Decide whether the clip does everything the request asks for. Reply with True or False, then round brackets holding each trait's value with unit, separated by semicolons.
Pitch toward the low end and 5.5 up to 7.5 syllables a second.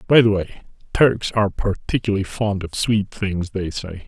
False (100 Hz; 5.0 syllables/s)